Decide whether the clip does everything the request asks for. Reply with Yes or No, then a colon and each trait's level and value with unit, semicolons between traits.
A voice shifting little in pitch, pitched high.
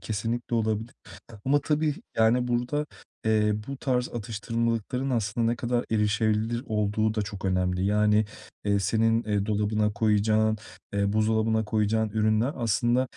No: narrow, 2.0 semitones; low, 110 Hz